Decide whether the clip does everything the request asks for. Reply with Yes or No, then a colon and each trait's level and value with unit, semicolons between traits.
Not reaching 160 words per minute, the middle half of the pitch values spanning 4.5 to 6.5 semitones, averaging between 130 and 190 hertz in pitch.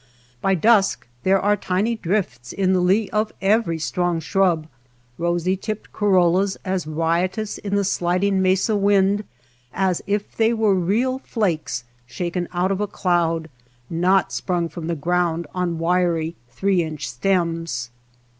No: average, 145 wpm; average, 2.9 semitones; medium, 185 Hz